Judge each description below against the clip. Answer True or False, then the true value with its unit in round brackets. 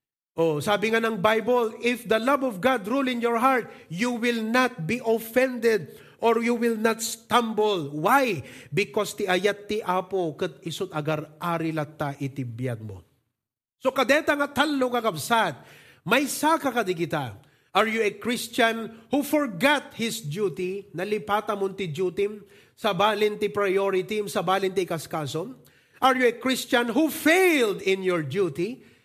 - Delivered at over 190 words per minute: False (150 wpm)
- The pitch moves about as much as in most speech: False (5.8 semitones)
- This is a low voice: False (210 Hz)